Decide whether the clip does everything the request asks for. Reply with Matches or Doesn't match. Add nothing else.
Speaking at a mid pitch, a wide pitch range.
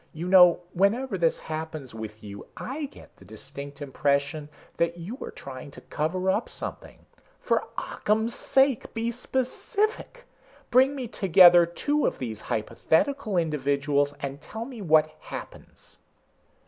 Matches